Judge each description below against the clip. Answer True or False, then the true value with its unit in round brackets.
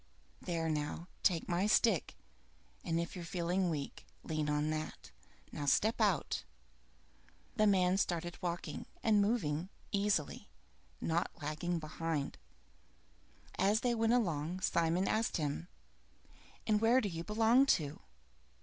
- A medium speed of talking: False (125 wpm)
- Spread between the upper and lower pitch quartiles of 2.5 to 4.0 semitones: False (4.7 semitones)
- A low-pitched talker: False (175 Hz)